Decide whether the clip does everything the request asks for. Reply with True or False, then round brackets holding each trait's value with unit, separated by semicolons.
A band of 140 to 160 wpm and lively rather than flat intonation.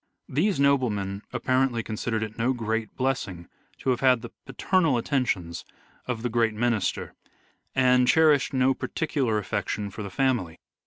False (145 wpm; 3.6 semitones)